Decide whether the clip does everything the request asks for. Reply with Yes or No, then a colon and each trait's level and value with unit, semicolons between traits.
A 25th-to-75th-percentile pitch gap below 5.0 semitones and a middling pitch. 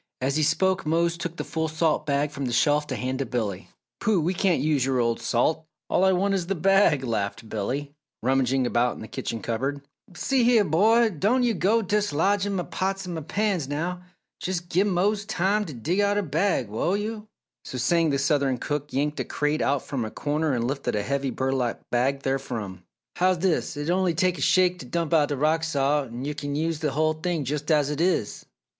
No: average, 5.3 semitones; medium, 155 Hz